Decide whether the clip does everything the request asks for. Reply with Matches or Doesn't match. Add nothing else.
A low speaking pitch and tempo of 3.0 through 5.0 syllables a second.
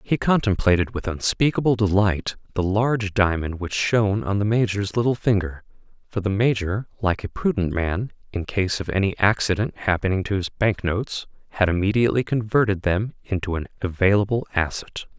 Doesn't match